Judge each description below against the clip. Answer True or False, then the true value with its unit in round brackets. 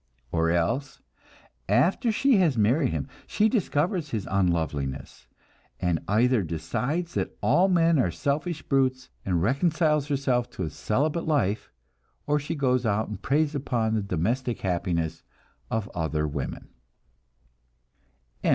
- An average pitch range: False (8.9 semitones)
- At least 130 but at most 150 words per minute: True (135 wpm)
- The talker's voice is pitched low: True (125 Hz)